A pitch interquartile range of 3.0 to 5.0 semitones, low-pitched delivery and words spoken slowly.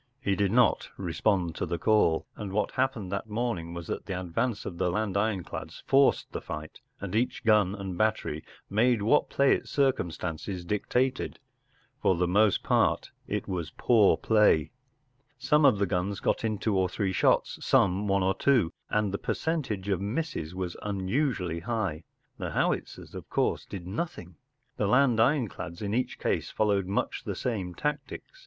No: average, 4.3 semitones; low, 100 Hz; average, 170 wpm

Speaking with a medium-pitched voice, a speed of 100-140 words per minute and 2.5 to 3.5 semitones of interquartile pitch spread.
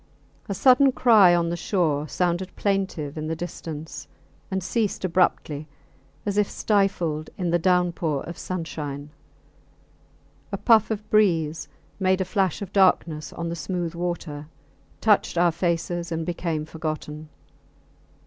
Yes: medium, 175 Hz; slow, 135 wpm; average, 3.2 semitones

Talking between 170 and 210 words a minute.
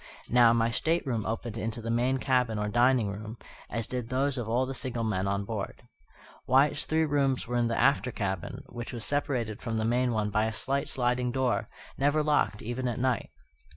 Yes: average, 200 wpm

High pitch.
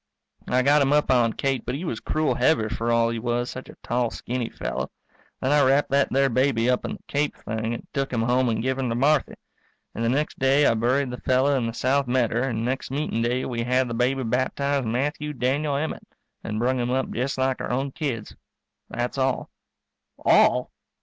No: low, 130 Hz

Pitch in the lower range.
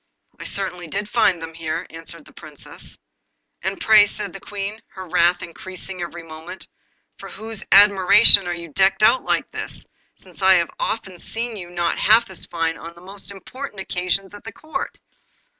No: high, 190 Hz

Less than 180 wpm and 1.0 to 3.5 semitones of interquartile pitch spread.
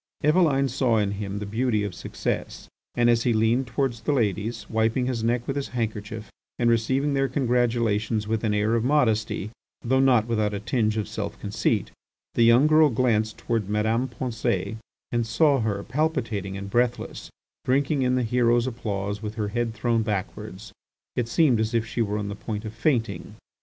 No: average, 185 wpm; average, 2.8 semitones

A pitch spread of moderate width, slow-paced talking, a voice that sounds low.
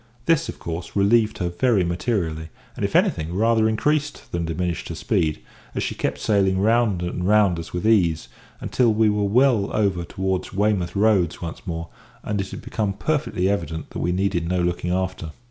No: average, 3.8 semitones; average, 185 wpm; very low, 95 Hz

